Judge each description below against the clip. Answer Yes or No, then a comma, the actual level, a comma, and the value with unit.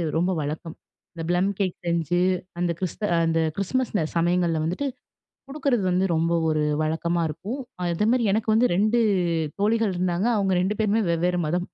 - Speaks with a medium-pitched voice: Yes, medium, 180 Hz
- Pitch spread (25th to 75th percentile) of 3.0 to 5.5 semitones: Yes, average, 3.9 semitones